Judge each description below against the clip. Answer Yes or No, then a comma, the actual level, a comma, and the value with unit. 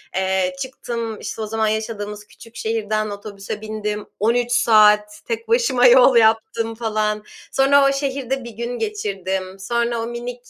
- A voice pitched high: Yes, high, 225 Hz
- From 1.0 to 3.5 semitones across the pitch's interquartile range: Yes, narrow, 2.6 semitones